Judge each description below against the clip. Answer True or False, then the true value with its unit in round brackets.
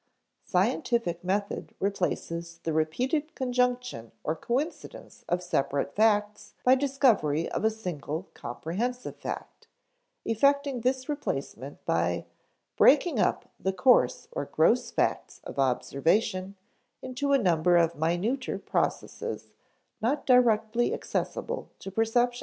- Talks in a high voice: True (220 Hz)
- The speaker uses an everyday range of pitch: False (6.7 semitones)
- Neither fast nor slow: False (110 wpm)